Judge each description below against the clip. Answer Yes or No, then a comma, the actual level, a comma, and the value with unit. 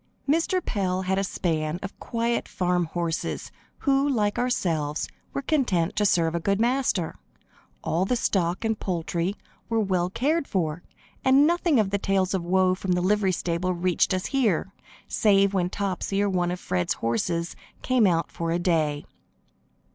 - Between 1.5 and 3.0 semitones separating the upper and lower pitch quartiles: No, average, 4.1 semitones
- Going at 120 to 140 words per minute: No, average, 165 wpm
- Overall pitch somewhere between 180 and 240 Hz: Yes, medium, 185 Hz